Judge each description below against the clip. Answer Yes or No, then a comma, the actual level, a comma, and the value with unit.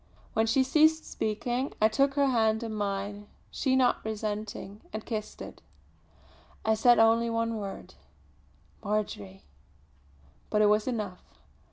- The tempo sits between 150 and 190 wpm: No, slow, 135 wpm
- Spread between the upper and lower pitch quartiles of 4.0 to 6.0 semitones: No, narrow, 2.5 semitones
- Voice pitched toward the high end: Yes, high, 220 Hz